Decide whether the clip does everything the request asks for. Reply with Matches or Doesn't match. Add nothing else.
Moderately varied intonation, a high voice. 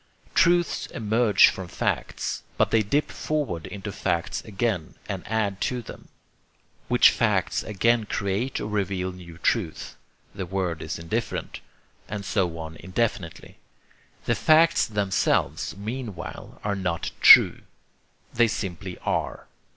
Doesn't match